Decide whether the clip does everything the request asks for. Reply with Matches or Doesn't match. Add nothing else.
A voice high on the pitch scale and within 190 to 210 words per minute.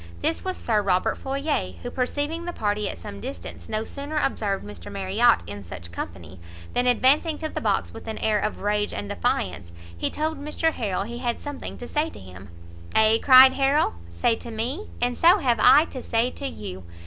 Matches